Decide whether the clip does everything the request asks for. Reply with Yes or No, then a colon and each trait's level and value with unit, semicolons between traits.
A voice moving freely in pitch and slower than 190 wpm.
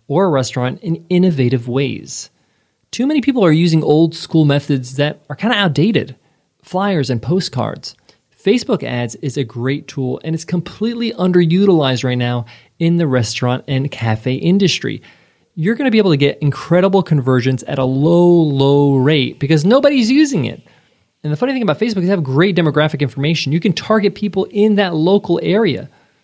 Yes: wide, 6.0 semitones; average, 180 wpm